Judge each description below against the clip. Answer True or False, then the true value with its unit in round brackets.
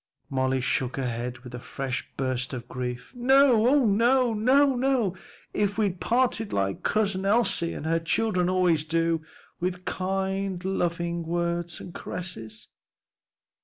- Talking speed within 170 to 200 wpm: False (135 wpm)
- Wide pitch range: True (8.0 semitones)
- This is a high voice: False (180 Hz)